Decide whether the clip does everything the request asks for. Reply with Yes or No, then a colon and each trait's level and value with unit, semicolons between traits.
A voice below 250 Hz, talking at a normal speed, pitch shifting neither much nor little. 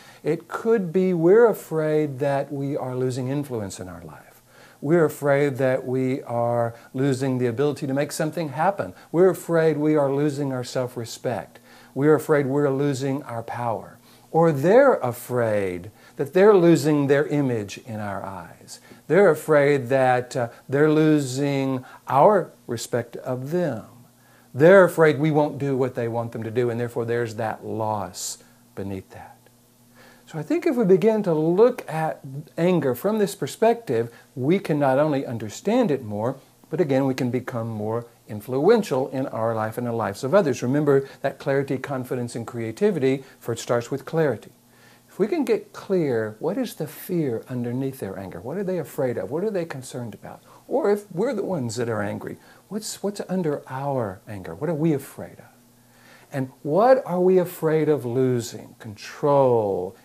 Yes: low, 135 Hz; average, 170 wpm; average, 4.8 semitones